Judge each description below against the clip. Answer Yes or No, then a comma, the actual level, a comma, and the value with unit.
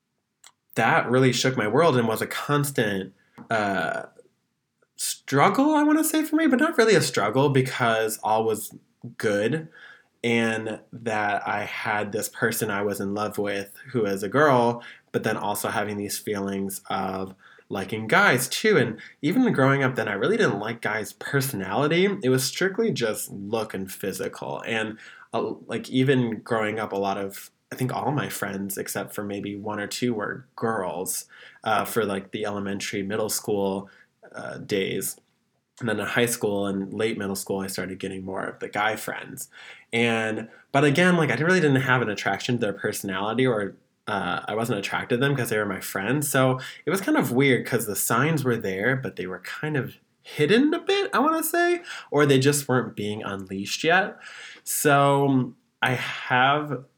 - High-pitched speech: No, low, 115 Hz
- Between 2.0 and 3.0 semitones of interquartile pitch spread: No, wide, 5.6 semitones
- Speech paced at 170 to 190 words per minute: Yes, average, 185 wpm